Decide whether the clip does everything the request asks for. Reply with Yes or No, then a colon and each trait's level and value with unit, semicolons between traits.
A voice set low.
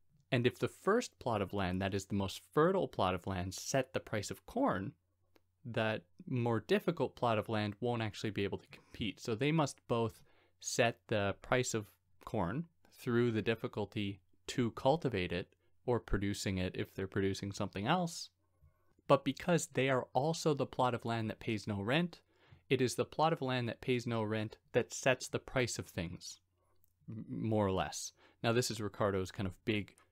Yes: low, 110 Hz